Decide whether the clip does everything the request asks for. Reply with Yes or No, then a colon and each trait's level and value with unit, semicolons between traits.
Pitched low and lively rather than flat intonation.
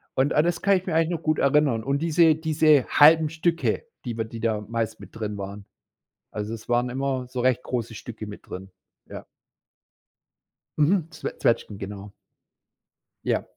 Yes: low, 130 Hz; wide, 6.1 semitones